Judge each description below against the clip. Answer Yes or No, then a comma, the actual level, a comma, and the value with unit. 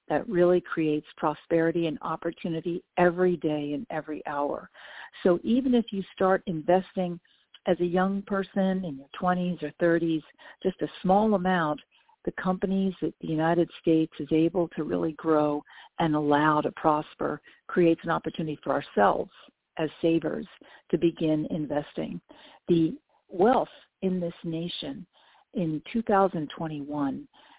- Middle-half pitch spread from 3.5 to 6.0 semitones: No, average, 3.0 semitones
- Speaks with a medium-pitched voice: Yes, medium, 170 Hz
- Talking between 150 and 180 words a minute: No, slow, 135 wpm